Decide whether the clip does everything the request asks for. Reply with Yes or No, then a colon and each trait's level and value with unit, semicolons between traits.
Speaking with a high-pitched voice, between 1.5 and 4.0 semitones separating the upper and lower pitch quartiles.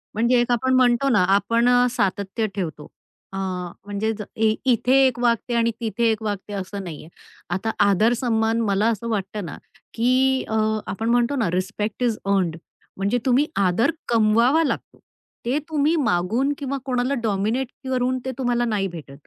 Yes: high, 230 Hz; average, 3.5 semitones